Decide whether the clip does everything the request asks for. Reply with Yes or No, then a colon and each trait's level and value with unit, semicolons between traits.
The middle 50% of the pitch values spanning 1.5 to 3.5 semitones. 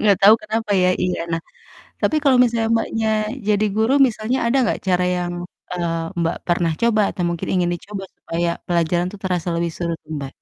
No: average, 4.2 semitones